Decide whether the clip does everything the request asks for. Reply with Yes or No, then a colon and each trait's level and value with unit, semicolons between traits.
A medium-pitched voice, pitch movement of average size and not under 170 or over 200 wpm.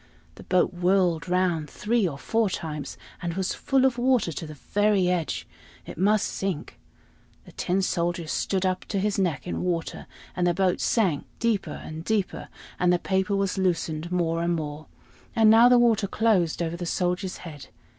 Yes: medium, 180 Hz; average, 3.2 semitones; average, 180 wpm